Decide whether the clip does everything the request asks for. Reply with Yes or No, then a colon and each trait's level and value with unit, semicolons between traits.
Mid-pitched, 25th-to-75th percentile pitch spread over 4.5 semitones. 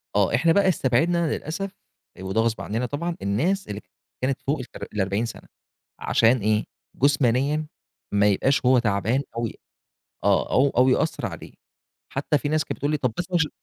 No: low, 130 Hz; average, 5.3 semitones